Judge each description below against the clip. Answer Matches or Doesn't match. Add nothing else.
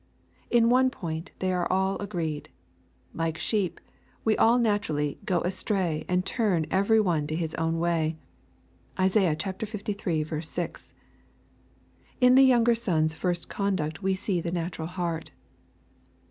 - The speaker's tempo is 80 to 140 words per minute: Matches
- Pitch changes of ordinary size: Matches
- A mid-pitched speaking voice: Matches